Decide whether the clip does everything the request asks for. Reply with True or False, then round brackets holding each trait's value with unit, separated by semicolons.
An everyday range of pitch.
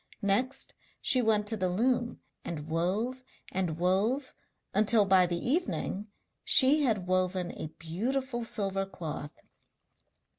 True (5.0 semitones)